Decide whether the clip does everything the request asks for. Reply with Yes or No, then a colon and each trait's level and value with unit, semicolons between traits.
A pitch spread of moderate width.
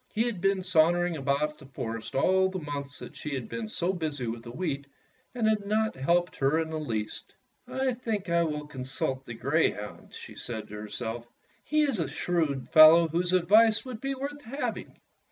No: wide, 6.6 semitones